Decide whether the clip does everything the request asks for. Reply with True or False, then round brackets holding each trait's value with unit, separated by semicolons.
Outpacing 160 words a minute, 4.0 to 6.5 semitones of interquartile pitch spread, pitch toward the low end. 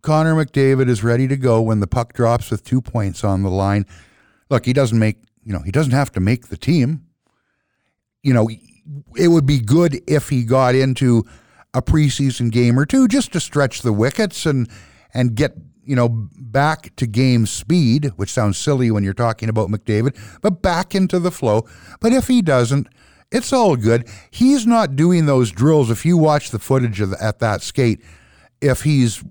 True (195 wpm; 5.3 semitones; 125 Hz)